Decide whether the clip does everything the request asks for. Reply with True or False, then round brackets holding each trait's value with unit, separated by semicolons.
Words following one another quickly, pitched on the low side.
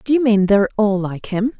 False (265 wpm; 215 Hz)